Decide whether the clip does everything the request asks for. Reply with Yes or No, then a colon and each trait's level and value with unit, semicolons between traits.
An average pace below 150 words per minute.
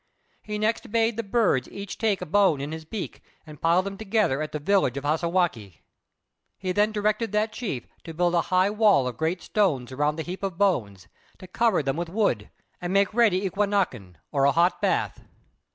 No: average, 200 wpm